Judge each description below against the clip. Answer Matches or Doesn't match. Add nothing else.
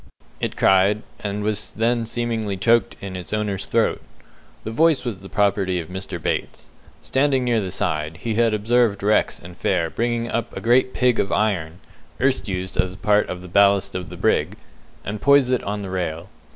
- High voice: Doesn't match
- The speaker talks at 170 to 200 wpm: Matches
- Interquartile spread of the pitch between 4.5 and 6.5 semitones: Doesn't match